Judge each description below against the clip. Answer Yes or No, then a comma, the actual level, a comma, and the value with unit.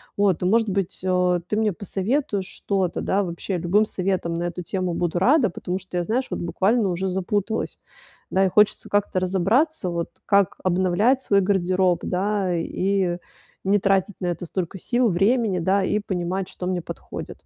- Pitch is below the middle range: No, high, 190 Hz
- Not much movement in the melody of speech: Yes, narrow, 2.3 semitones